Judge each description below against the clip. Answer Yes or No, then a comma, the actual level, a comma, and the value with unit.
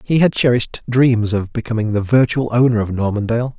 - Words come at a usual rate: Yes, average, 185 wpm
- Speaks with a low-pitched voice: Yes, low, 115 Hz